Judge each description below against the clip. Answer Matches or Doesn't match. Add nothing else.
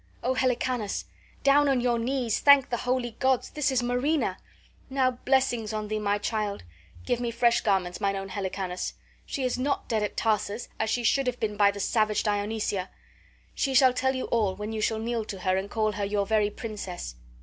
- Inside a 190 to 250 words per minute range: Matches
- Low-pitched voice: Doesn't match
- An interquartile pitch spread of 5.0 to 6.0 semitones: Doesn't match